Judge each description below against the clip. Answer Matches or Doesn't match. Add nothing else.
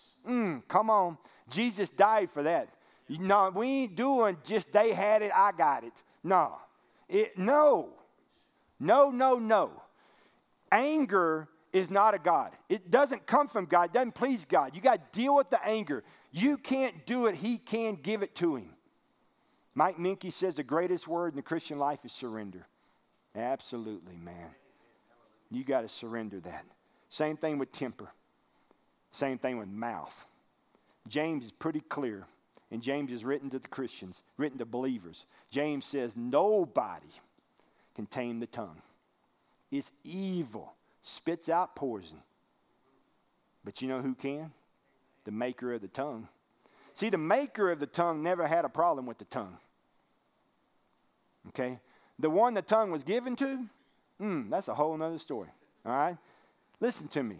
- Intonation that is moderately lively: Doesn't match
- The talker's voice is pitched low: Doesn't match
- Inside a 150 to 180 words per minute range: Matches